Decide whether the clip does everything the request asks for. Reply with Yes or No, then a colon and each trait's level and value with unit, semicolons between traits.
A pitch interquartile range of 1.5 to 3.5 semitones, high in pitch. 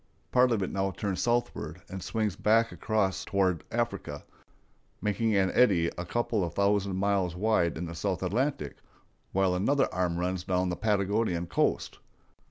No: average, 3.2 semitones; very low, 95 Hz